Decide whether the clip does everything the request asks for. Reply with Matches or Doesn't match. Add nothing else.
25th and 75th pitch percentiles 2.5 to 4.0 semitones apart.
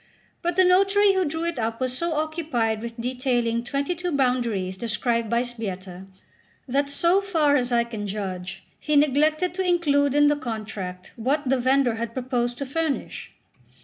Doesn't match